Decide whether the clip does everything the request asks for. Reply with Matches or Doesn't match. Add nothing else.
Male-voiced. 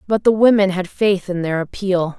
Doesn't match